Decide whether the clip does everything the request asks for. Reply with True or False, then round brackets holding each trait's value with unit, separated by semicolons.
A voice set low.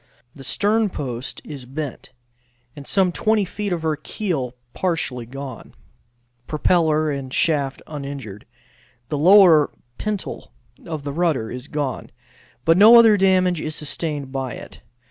False (155 Hz)